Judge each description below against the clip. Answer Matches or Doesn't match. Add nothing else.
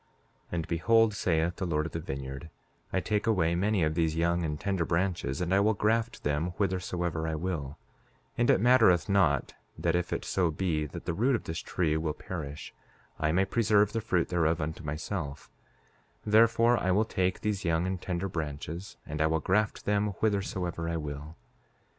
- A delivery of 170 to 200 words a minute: Matches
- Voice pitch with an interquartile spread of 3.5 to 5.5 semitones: Matches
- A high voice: Doesn't match